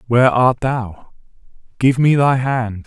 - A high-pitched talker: No, low, 125 Hz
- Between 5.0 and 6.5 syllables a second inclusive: No, 4.0 syllables/s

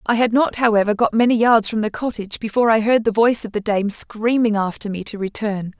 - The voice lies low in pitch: No, high, 220 Hz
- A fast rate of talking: Yes, fast, 240 wpm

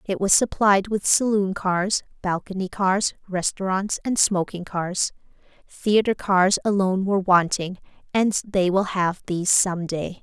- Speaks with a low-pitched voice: No, high, 190 Hz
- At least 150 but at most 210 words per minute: No, average, 140 wpm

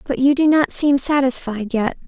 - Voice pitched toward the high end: Yes, very high, 265 Hz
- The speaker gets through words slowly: No, average, 200 wpm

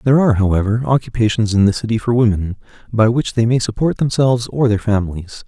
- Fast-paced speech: No, average, 195 wpm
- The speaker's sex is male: Yes, male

